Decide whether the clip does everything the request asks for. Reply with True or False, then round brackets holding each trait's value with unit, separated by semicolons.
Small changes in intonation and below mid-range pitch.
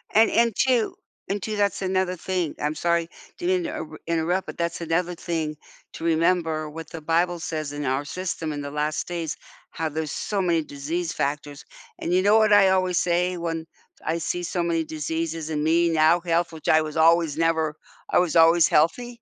False (2.3 semitones; 165 Hz)